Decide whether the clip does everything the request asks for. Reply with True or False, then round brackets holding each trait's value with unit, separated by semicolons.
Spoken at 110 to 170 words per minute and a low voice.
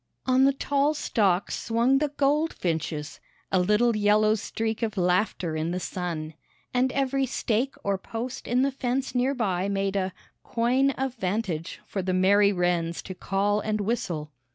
False (160 wpm; 210 Hz)